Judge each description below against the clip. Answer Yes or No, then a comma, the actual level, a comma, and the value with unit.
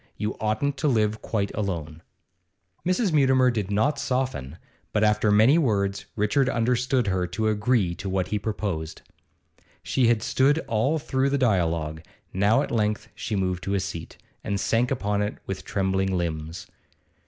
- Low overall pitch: Yes, low, 105 Hz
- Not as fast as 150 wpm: No, average, 160 wpm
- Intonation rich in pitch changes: No, average, 4.7 semitones